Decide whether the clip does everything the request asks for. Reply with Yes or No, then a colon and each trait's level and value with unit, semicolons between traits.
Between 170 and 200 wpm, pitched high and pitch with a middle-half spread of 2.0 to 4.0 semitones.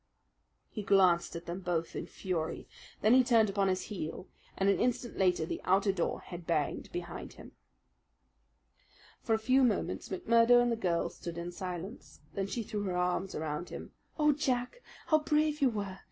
No: average, 180 wpm; high, 195 Hz; average, 5.1 semitones